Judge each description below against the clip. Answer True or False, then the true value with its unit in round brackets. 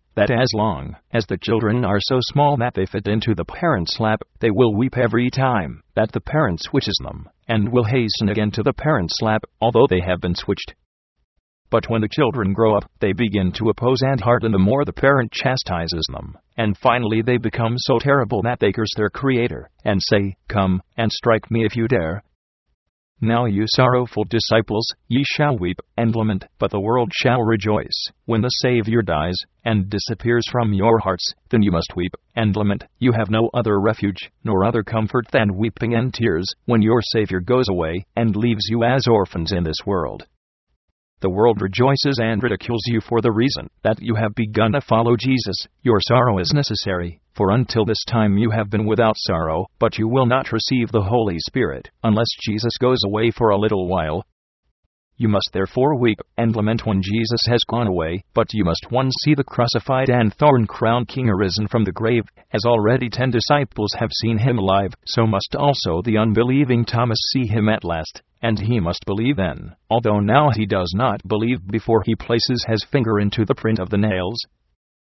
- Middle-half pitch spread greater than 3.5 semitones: False (3.2 semitones)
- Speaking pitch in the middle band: False (110 Hz)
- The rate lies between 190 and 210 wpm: True (195 wpm)